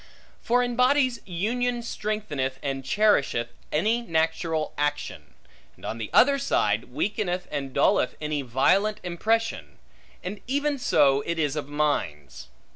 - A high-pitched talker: No, medium, 170 Hz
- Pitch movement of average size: No, wide, 8.1 semitones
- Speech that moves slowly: Yes, slow, 130 wpm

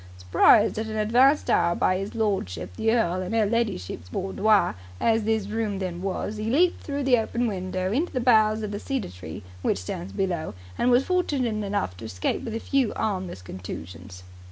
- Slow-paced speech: No, average, 190 wpm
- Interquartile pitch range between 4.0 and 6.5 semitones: Yes, average, 4.9 semitones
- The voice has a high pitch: Yes, high, 210 Hz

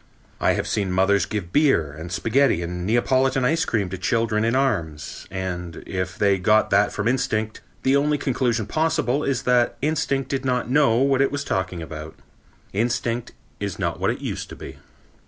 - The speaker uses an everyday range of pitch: No, wide, 6.1 semitones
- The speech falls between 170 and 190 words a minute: Yes, average, 180 wpm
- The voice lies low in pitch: Yes, low, 115 Hz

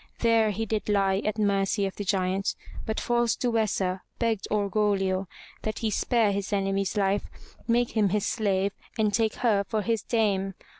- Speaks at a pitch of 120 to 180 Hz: No, high, 205 Hz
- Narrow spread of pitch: Yes, narrow, 2.2 semitones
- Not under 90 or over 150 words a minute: No, average, 165 wpm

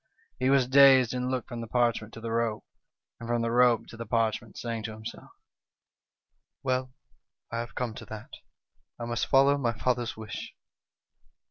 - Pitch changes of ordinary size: No, narrow, 1.9 semitones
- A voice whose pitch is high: No, low, 120 Hz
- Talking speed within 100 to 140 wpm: No, average, 175 wpm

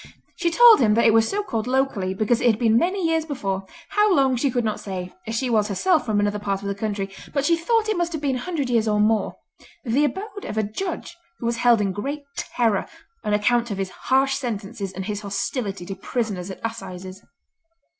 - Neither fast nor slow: No, fast, 220 wpm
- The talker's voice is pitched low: No, high, 230 Hz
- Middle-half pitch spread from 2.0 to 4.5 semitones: No, wide, 5.6 semitones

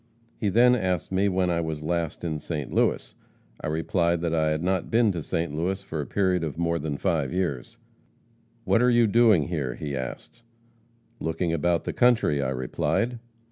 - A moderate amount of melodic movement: Yes, average, 3.7 semitones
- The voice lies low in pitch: Yes, very low, 85 Hz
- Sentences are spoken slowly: No, average, 185 wpm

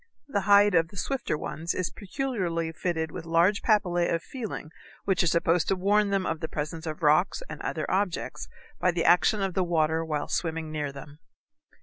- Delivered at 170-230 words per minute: Yes, average, 195 wpm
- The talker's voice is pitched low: No, medium, 175 Hz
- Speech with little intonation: No, average, 3.5 semitones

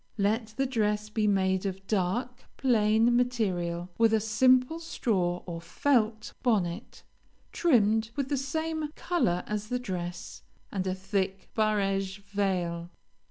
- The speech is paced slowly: Yes, slow, 130 wpm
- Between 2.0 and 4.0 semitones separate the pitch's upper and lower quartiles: No, average, 4.4 semitones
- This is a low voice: No, high, 210 Hz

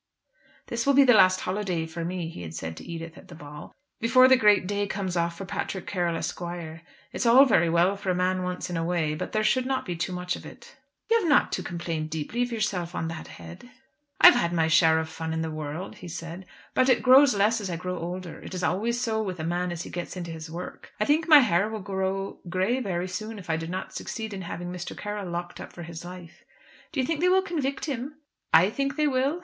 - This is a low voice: No, medium, 185 Hz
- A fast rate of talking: Yes, fast, 255 wpm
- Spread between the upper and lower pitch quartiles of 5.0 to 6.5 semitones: Yes, average, 5.3 semitones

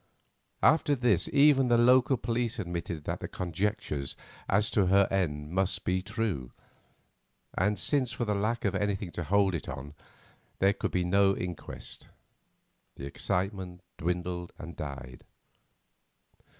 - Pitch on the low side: Yes, very low, 95 Hz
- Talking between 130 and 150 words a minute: Yes, slow, 135 wpm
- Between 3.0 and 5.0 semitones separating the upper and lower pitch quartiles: Yes, average, 3.7 semitones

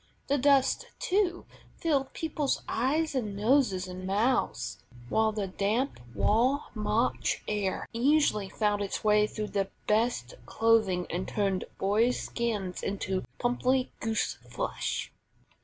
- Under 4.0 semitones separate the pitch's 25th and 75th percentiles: No, average, 4.8 semitones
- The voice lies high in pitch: Yes, high, 220 Hz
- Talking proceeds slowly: Yes, slow, 125 wpm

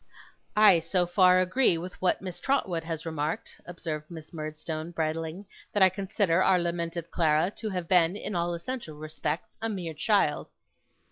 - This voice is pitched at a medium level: Yes, medium, 170 Hz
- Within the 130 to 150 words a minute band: No, average, 160 wpm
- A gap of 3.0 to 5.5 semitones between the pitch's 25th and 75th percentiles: No, narrow, 2.6 semitones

